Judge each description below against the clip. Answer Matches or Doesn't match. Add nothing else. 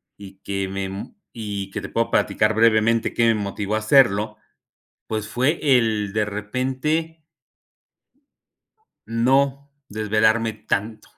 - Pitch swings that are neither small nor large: Doesn't match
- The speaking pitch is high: Doesn't match